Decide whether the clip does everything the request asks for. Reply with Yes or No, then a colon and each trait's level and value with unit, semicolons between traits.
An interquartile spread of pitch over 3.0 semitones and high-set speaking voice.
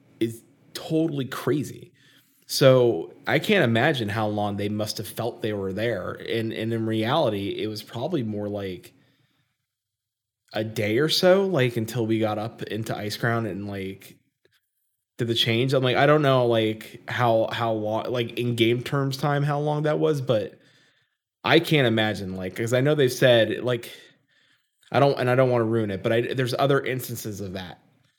No: average, 3.7 semitones; low, 115 Hz